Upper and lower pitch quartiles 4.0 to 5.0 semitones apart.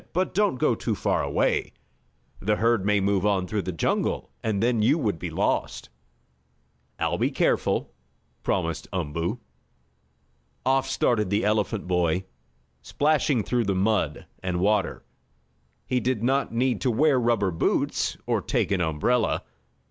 Yes: average, 4.7 semitones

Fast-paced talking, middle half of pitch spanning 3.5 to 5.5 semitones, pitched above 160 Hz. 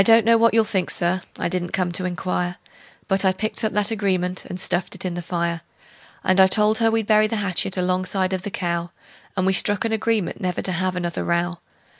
No: fast, 230 wpm; average, 2.9 semitones; medium, 185 Hz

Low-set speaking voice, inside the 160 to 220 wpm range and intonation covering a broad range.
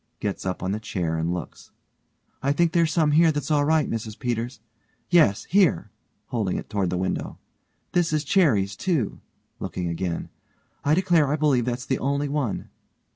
Yes: low, 130 Hz; average, 175 wpm; wide, 7.6 semitones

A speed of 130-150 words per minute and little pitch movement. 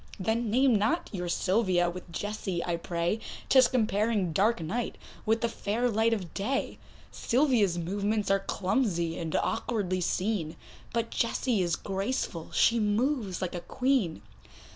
No: average, 140 wpm; average, 4.6 semitones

